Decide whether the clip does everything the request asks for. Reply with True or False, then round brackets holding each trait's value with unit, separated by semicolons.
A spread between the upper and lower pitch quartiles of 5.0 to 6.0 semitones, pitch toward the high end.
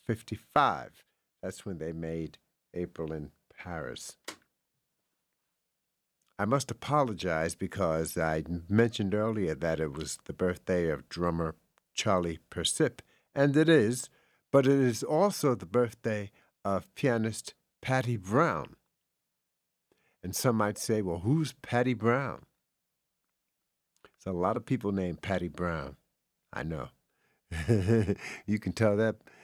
False (5.6 semitones; 105 Hz)